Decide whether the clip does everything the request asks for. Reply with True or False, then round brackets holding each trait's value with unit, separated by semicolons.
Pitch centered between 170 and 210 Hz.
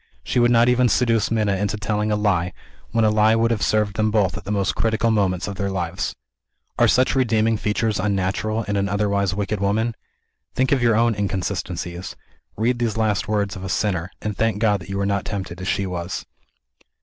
False (105 Hz)